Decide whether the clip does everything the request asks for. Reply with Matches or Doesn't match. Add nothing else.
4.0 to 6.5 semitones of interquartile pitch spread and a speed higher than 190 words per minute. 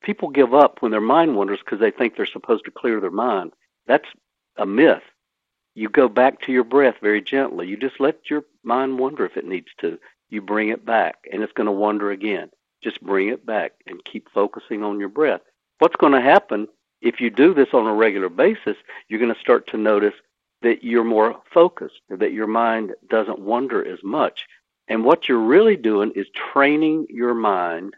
Matches